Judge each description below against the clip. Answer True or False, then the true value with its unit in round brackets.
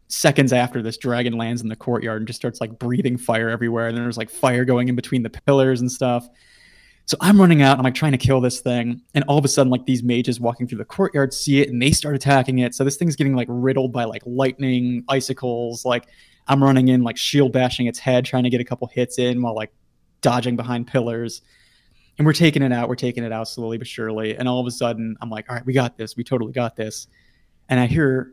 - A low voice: True (125 Hz)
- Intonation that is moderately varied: False (2.0 semitones)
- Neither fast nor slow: False (255 wpm)